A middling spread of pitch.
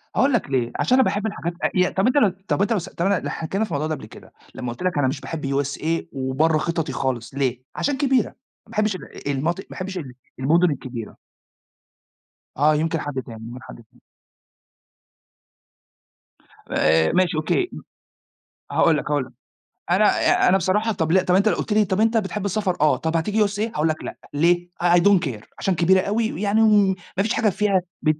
No: wide, 5.7 semitones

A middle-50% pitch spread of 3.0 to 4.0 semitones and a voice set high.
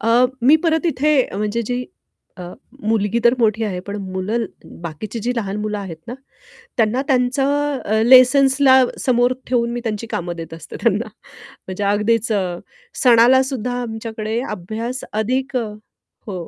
Yes: average, 3.6 semitones; high, 230 Hz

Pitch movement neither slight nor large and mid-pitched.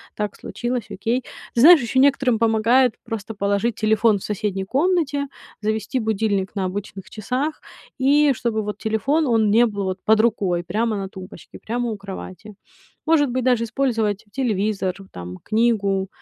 No: average, 3.7 semitones; high, 220 Hz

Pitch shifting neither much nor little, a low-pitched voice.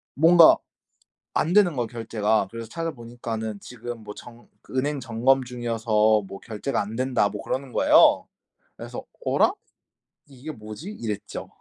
Yes: average, 3.5 semitones; low, 120 Hz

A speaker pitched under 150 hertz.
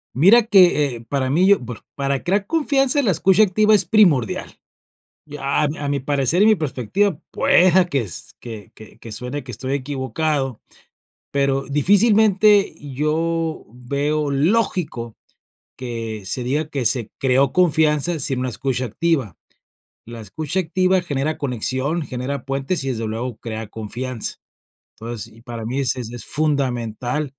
Yes: medium, 140 Hz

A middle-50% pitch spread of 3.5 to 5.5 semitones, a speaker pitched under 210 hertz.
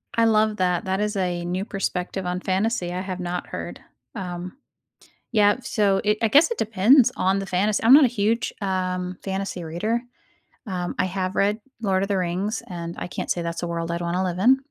No: average, 2.9 semitones; high, 190 Hz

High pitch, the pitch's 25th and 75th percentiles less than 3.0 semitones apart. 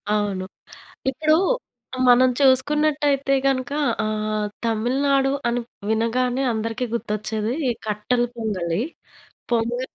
No: high, 240 Hz; average, 3.7 semitones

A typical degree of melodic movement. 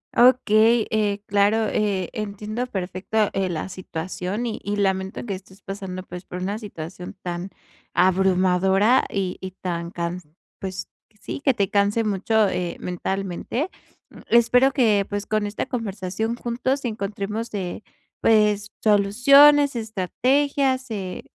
Yes: average, 3.3 semitones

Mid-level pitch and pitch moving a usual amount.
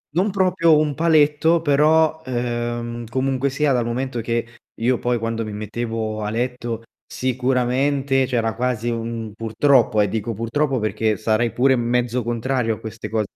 No: low, 120 Hz; average, 3.0 semitones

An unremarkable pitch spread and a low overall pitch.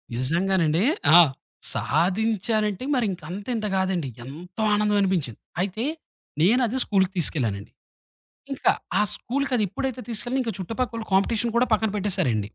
No: average, 4.4 semitones; high, 200 Hz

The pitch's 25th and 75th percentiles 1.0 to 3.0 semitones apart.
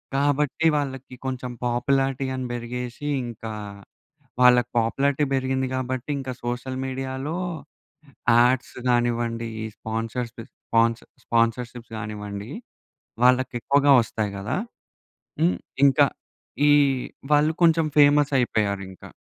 Yes: narrow, 2.6 semitones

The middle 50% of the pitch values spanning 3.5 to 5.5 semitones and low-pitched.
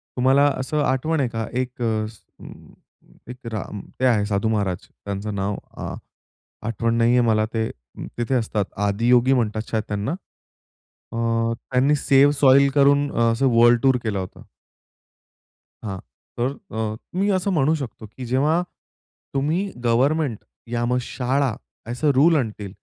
Yes: average, 4.0 semitones; low, 125 Hz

